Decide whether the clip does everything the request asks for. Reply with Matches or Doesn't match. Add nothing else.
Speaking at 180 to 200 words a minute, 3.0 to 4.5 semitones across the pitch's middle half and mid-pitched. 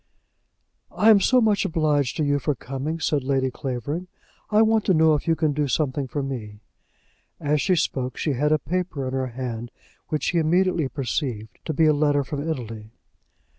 Matches